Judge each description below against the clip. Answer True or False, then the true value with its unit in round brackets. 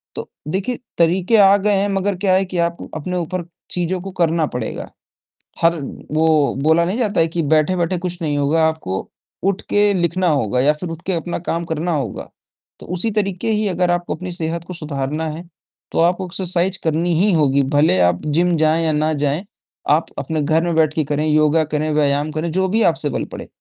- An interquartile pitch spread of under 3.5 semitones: True (3.0 semitones)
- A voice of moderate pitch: True (165 Hz)